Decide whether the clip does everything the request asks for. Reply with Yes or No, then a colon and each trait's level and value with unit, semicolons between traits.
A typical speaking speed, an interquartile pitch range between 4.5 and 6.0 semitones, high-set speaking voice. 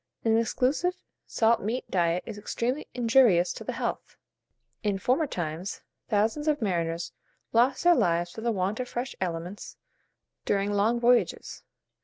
Yes: average, 150 wpm; average, 5.2 semitones; high, 220 Hz